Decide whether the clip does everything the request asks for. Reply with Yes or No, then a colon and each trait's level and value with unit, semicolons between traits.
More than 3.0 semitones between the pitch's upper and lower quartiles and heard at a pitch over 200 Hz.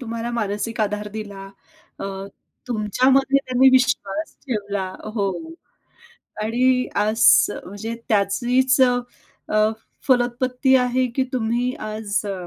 Yes: average, 3.5 semitones; high, 235 Hz